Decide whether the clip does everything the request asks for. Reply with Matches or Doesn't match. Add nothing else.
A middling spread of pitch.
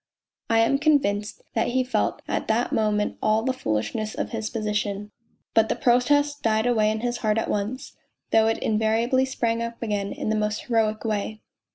Doesn't match